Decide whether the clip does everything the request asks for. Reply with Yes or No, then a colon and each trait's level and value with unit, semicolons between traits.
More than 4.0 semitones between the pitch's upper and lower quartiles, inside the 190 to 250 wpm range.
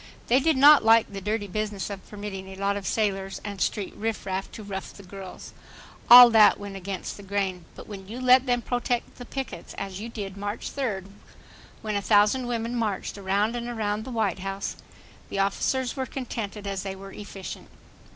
No: average, 3.1 semitones; average, 195 wpm